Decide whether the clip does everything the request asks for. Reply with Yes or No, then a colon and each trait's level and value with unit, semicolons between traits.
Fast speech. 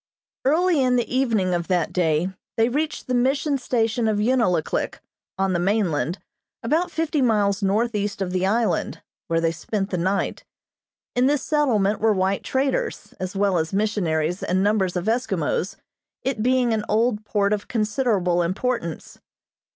No: average, 155 wpm